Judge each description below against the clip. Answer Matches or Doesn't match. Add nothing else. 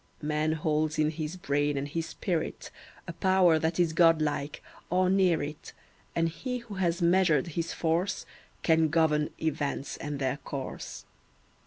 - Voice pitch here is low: Doesn't match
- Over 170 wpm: Doesn't match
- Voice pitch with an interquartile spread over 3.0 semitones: Doesn't match